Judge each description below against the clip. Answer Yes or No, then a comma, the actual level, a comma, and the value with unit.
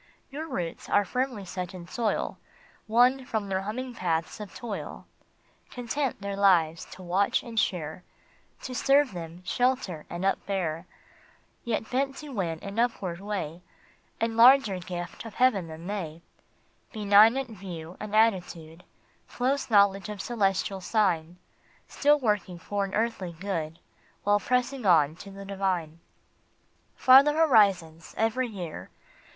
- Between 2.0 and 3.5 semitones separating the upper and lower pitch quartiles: No, average, 5.0 semitones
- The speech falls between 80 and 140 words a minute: Yes, slow, 135 wpm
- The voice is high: Yes, high, 200 Hz